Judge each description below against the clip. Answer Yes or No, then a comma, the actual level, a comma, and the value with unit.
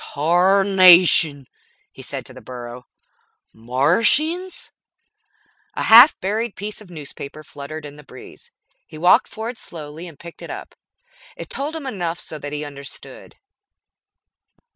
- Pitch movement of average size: No, wide, 6.4 semitones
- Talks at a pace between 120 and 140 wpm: Yes, slow, 135 wpm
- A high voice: No, medium, 170 Hz